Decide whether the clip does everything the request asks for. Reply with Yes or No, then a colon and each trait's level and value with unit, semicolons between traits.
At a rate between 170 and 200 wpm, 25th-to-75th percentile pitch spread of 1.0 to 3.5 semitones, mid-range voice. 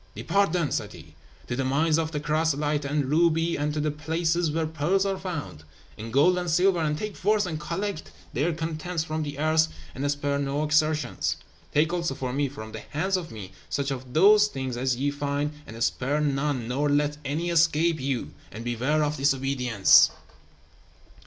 Yes: average, 185 wpm; average, 3.0 semitones; medium, 150 Hz